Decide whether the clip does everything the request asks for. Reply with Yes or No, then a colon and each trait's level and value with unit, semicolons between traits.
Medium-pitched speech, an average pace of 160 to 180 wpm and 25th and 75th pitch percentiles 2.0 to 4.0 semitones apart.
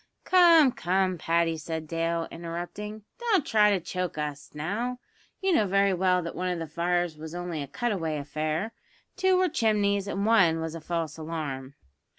No: medium, 175 Hz; average, 175 wpm; average, 4.5 semitones